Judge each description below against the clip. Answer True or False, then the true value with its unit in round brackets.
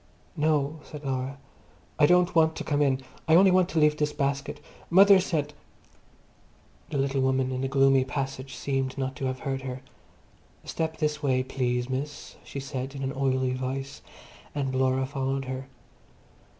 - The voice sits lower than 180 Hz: True (135 Hz)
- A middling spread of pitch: False (2.2 semitones)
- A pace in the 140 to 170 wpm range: True (165 wpm)